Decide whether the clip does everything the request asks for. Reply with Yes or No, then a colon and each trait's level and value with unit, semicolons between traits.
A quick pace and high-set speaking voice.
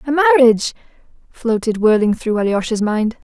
No: slow, 125 wpm; high, 235 Hz